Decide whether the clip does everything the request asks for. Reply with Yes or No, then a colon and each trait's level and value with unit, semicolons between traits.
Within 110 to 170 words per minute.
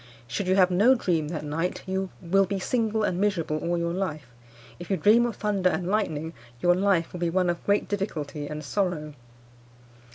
No: average, 195 wpm